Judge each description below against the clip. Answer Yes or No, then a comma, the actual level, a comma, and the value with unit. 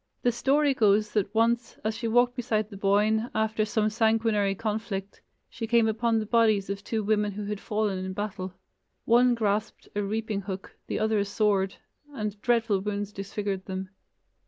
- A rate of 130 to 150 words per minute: No, average, 175 wpm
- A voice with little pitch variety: Yes, narrow, 2.0 semitones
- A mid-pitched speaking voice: No, high, 215 Hz